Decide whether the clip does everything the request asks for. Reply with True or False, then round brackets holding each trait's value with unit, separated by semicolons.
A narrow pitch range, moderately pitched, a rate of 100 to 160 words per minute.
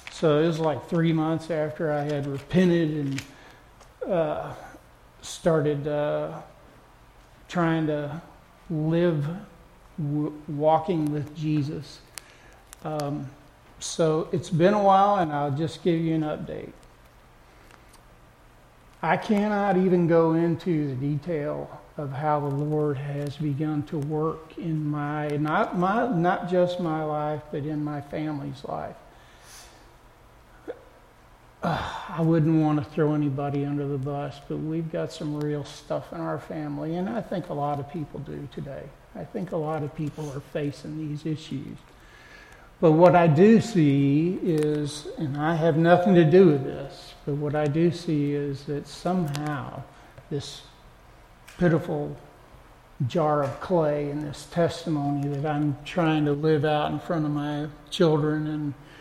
True (2.3 semitones; 150 Hz; 145 wpm)